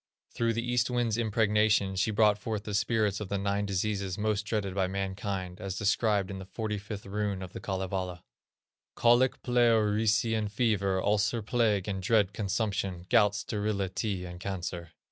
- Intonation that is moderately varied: No, narrow, 2.1 semitones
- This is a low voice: Yes, low, 105 Hz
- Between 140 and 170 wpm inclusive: Yes, average, 160 wpm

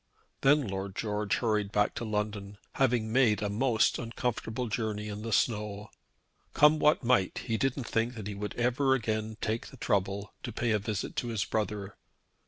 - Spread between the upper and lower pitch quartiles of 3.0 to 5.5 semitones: No, narrow, 2.6 semitones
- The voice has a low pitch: Yes, low, 110 Hz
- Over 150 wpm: Yes, average, 180 wpm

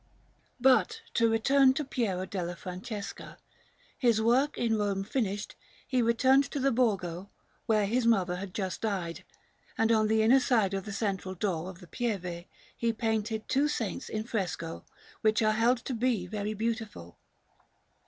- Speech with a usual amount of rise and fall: Yes, average, 3.7 semitones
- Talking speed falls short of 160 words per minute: No, average, 165 wpm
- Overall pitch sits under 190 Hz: No, high, 220 Hz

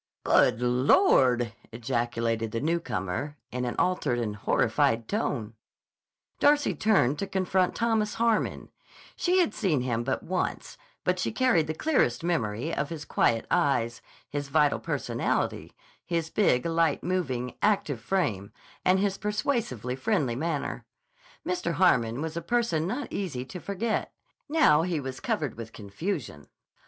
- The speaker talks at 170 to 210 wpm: No, average, 140 wpm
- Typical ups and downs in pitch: No, wide, 7.9 semitones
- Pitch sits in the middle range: Yes, medium, 150 Hz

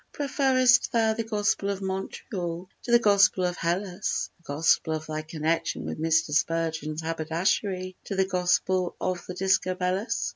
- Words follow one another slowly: No, average, 150 wpm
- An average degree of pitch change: Yes, average, 3.4 semitones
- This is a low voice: No, medium, 185 Hz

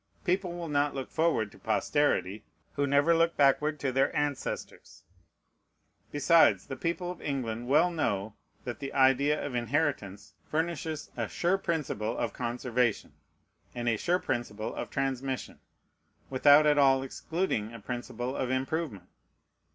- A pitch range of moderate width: Yes, average, 4.5 semitones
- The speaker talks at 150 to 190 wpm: No, average, 140 wpm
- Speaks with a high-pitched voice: No, low, 135 Hz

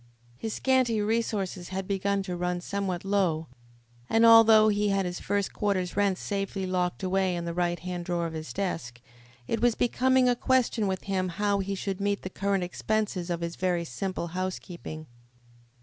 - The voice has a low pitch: No, high, 190 Hz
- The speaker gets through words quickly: No, average, 180 wpm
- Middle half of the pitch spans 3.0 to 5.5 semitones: No, narrow, 2.6 semitones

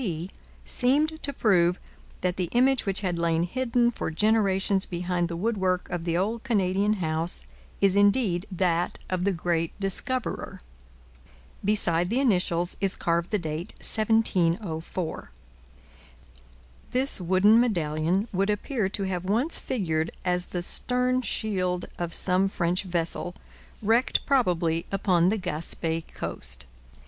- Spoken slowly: Yes, slow, 130 wpm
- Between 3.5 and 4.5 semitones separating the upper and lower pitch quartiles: Yes, average, 4.0 semitones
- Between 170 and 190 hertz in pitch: Yes, medium, 185 Hz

